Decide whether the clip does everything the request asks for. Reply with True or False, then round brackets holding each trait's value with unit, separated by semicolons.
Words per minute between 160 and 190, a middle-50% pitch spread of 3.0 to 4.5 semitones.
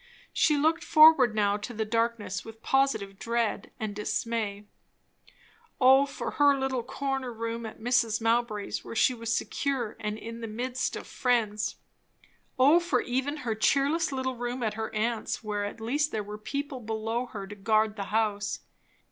True (165 wpm; 3.4 semitones)